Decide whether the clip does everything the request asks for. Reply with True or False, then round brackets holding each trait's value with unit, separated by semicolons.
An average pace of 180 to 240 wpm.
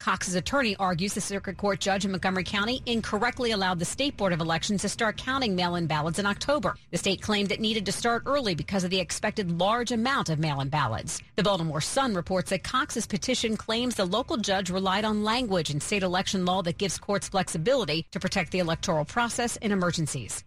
True (205 wpm)